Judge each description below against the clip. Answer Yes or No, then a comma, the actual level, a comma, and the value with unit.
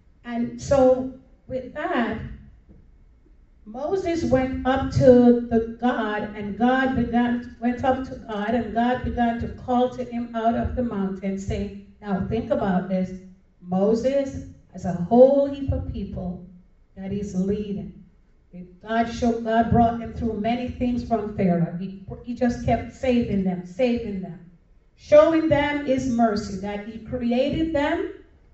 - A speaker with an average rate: Yes, average, 145 wpm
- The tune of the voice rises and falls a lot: No, average, 4.2 semitones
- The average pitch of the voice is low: No, high, 235 Hz